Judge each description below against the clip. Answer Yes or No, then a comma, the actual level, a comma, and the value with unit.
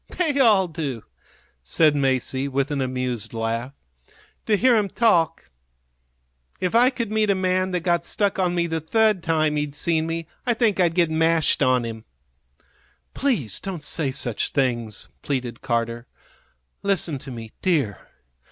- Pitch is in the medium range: Yes, medium, 160 Hz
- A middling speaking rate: Yes, average, 155 wpm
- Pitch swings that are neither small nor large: No, wide, 6.6 semitones